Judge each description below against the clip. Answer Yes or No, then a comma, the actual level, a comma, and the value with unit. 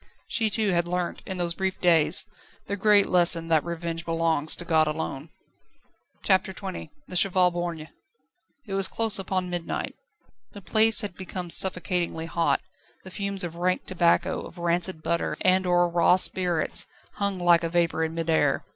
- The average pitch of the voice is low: No, medium, 175 Hz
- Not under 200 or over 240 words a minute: No, average, 165 wpm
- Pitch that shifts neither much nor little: No, narrow, 2.1 semitones